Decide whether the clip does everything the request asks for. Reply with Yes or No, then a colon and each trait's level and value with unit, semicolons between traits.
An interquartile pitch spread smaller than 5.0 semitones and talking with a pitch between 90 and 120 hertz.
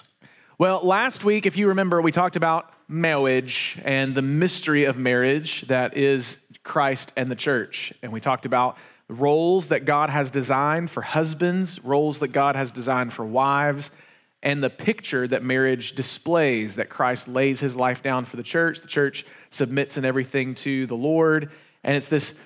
No: average, 3.6 semitones; medium, 140 Hz